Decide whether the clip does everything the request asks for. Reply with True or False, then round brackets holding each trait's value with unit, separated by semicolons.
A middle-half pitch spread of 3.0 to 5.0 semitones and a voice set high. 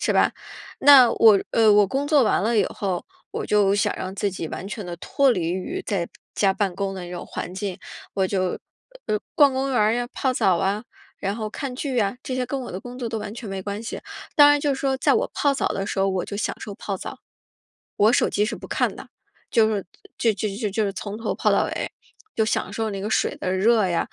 True (3.9 semitones; 210 Hz)